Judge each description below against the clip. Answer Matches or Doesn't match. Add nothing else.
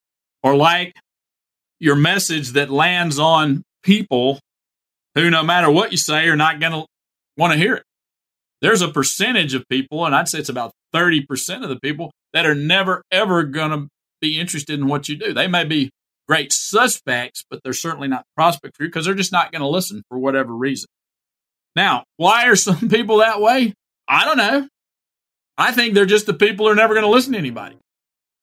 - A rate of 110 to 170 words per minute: Doesn't match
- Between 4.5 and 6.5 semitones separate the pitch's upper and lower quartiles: Matches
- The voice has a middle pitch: Matches